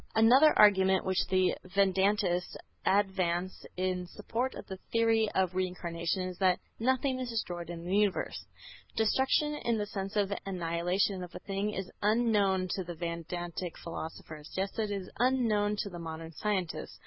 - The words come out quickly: No, average, 160 wpm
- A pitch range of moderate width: Yes, average, 3.0 semitones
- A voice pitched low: No, high, 190 Hz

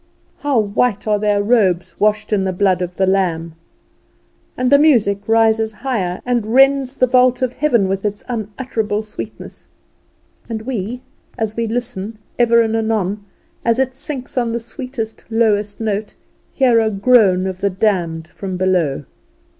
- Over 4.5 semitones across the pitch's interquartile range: No, average, 3.8 semitones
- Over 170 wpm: No, average, 155 wpm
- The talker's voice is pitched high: Yes, high, 220 Hz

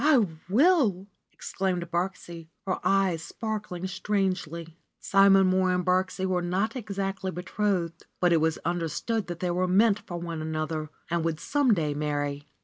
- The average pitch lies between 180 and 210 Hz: Yes, medium, 185 Hz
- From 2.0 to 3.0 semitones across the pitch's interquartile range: Yes, average, 2.7 semitones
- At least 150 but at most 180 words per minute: Yes, average, 155 wpm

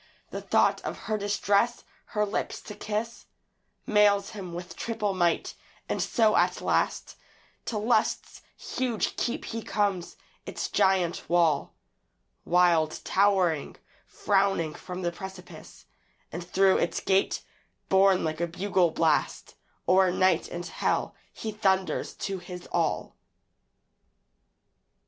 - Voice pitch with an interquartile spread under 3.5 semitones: Yes, average, 2.9 semitones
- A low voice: No, high, 190 Hz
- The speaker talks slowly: Yes, slow, 120 wpm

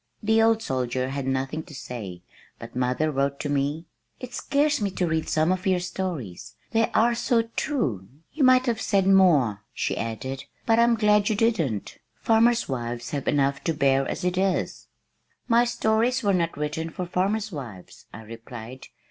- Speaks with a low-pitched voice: No, medium, 165 Hz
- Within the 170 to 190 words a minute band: Yes, average, 175 wpm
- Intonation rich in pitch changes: Yes, wide, 8.9 semitones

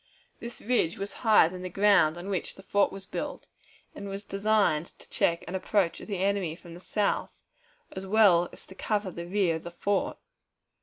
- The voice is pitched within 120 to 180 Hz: No, high, 195 Hz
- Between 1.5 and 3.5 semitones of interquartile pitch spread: Yes, average, 2.7 semitones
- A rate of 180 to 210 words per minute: Yes, average, 200 wpm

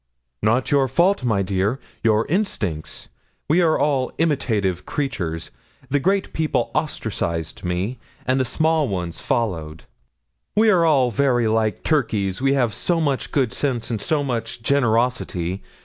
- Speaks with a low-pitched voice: Yes, low, 125 Hz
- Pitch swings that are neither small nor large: No, wide, 6.2 semitones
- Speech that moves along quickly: No, average, 140 wpm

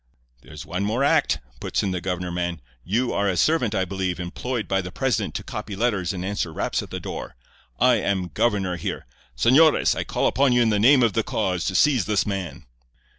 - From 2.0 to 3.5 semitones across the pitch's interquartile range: No, average, 4.5 semitones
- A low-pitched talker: Yes, low, 100 Hz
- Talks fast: Yes, fast, 215 wpm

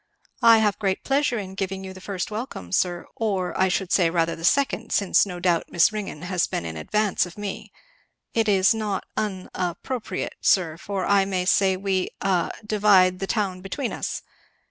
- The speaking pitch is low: No, high, 190 Hz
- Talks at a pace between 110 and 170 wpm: No, average, 190 wpm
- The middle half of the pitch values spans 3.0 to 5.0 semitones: No, narrow, 2.6 semitones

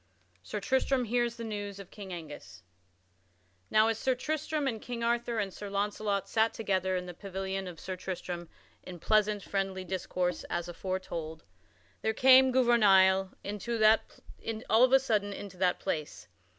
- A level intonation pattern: No, average, 3.7 semitones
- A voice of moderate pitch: No, high, 205 Hz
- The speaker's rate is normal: Yes, average, 150 wpm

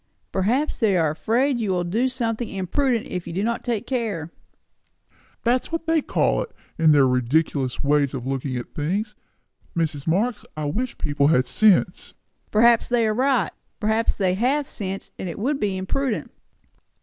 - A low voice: No, high, 205 Hz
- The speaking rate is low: No, average, 170 wpm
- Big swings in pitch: Yes, wide, 7.1 semitones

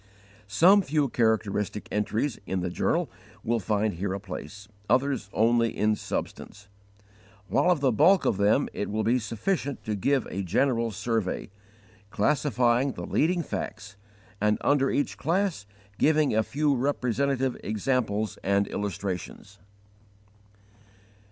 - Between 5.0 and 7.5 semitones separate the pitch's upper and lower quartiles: Yes, average, 5.3 semitones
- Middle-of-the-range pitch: No, low, 115 Hz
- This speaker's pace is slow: Yes, slow, 130 wpm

